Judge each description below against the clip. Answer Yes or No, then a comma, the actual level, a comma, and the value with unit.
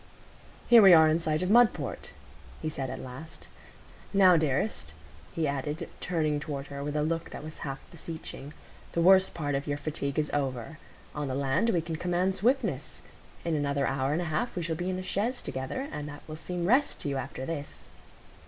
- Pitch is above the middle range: No, medium, 155 Hz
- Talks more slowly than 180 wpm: No, average, 200 wpm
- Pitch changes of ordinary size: Yes, average, 3.9 semitones